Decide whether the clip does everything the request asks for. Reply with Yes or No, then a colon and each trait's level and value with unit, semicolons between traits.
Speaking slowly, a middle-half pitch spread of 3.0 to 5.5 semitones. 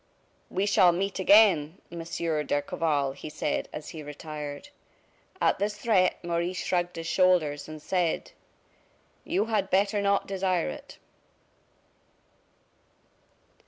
Yes: slow, 115 wpm; average, 4.1 semitones